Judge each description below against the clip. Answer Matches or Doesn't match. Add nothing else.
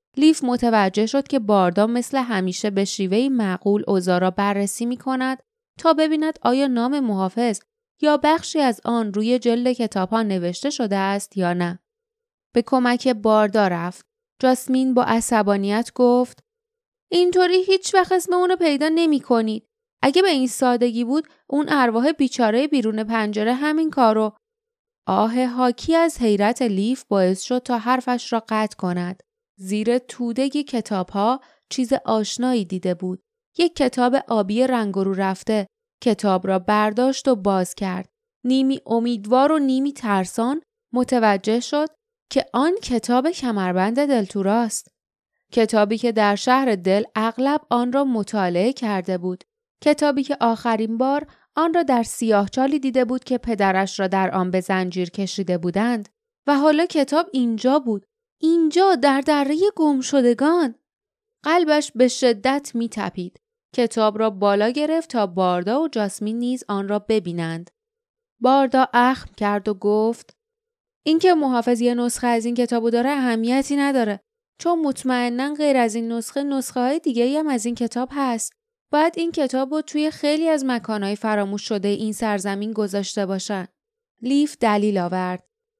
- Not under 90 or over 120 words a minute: Doesn't match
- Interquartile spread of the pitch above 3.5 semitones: Matches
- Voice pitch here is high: Matches